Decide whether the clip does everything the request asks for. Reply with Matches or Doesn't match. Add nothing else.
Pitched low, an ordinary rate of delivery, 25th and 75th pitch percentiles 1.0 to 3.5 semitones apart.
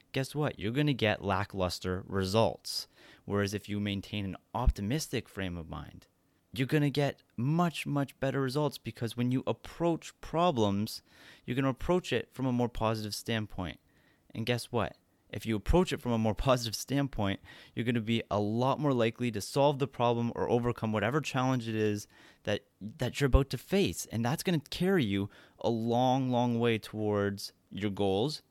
Doesn't match